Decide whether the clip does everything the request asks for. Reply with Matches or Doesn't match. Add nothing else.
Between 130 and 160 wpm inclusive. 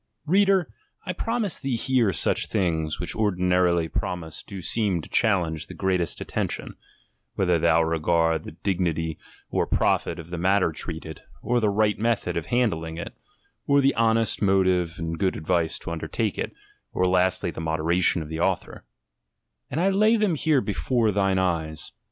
Doesn't match